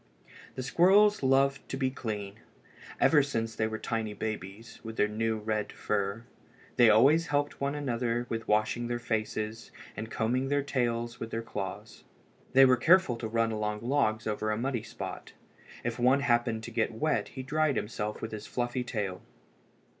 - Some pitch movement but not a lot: Yes, average, 3.4 semitones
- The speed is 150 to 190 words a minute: Yes, average, 170 wpm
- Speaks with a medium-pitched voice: No, low, 115 Hz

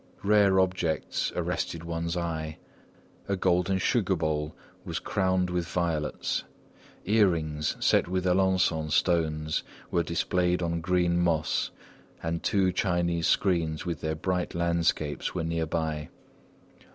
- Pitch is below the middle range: Yes, very low, 85 Hz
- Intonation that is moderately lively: No, narrow, 2.3 semitones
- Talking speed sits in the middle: No, slow, 120 wpm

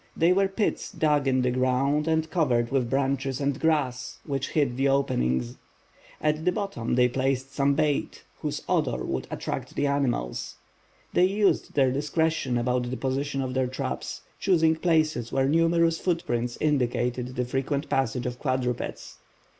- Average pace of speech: Yes, average, 155 wpm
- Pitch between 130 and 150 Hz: Yes, low, 135 Hz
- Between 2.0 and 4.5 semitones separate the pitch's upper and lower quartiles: Yes, average, 3.7 semitones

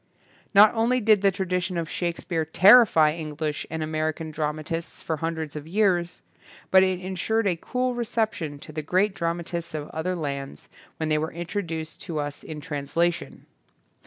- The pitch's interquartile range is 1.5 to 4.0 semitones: Yes, average, 3.4 semitones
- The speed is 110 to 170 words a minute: Yes, average, 160 wpm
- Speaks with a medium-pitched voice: Yes, medium, 165 Hz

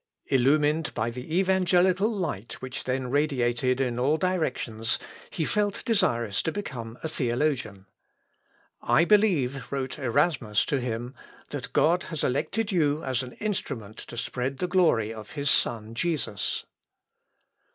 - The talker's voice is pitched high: No, low, 135 Hz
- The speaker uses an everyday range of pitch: No, wide, 6.2 semitones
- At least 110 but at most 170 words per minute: Yes, slow, 135 wpm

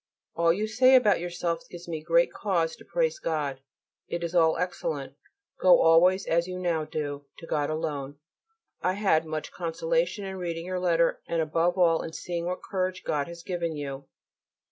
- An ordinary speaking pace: Yes, average, 180 wpm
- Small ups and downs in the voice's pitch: Yes, narrow, 2.3 semitones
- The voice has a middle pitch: Yes, medium, 170 Hz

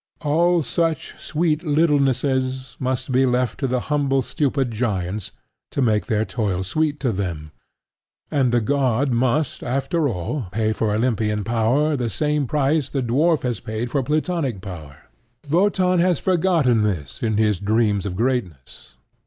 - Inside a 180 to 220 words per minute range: No, average, 150 wpm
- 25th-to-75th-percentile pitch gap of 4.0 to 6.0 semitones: Yes, wide, 5.4 semitones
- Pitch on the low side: Yes, low, 130 Hz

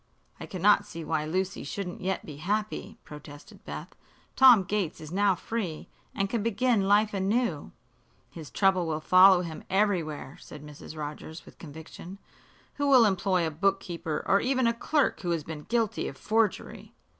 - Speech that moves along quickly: No, average, 165 wpm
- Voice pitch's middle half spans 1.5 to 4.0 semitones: No, average, 4.6 semitones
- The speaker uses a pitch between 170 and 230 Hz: Yes, high, 190 Hz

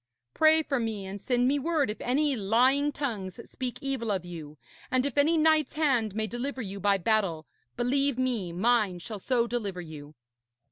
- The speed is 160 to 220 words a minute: Yes, average, 180 wpm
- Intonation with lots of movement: Yes, wide, 5.7 semitones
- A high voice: Yes, high, 240 Hz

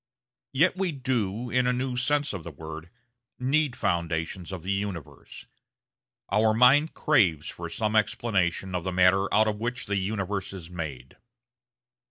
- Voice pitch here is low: Yes, low, 100 Hz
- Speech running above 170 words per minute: No, average, 155 wpm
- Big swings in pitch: Yes, wide, 6.1 semitones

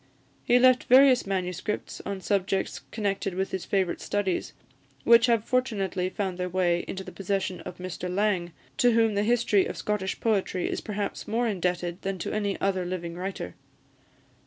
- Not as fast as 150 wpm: No, average, 165 wpm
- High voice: Yes, high, 195 Hz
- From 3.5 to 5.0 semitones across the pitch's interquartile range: No, average, 2.7 semitones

